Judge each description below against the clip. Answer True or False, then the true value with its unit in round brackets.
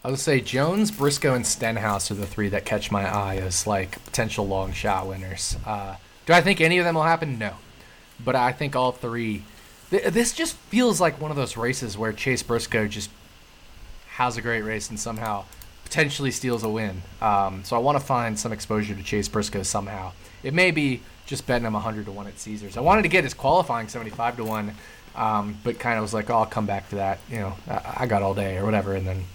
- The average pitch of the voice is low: True (110 Hz)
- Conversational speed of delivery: False (230 wpm)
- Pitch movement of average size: True (4.0 semitones)